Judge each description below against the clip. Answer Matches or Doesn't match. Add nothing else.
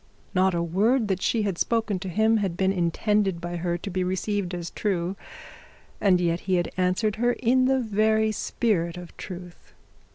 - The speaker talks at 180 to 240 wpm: Matches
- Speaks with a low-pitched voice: Doesn't match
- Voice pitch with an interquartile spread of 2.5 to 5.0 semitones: Matches